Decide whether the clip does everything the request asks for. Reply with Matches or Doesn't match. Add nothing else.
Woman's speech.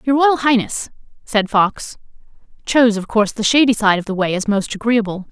Matches